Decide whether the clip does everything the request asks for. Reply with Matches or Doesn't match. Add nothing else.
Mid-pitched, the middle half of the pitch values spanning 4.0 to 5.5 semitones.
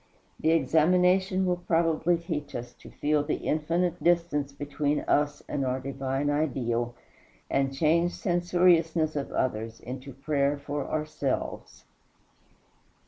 Doesn't match